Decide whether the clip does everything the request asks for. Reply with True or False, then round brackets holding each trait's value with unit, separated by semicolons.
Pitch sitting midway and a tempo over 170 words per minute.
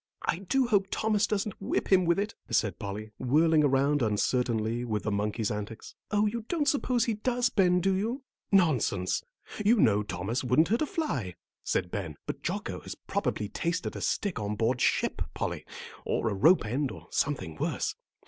True (145 Hz; 180 wpm)